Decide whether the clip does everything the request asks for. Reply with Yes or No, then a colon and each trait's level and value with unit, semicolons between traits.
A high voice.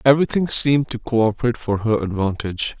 No: low, 120 Hz